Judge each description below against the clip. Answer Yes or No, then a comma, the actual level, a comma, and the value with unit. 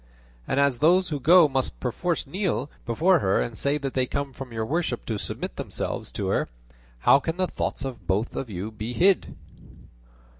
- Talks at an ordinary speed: Yes, average, 185 wpm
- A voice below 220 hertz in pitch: Yes, low, 135 Hz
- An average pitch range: No, wide, 6.0 semitones